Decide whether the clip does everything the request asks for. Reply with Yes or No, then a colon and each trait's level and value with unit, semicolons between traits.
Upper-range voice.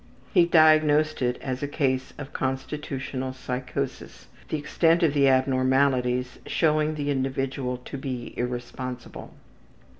No: low, 135 Hz